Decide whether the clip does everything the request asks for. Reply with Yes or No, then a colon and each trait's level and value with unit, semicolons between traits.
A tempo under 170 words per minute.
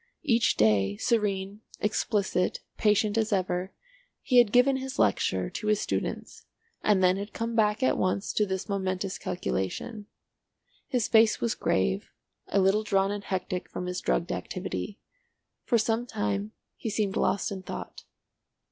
Yes: average, 150 wpm